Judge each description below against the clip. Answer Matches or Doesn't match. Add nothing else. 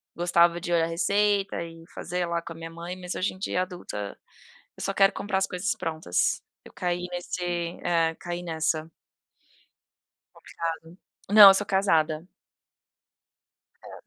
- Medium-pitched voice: Matches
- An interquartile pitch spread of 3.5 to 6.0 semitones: Doesn't match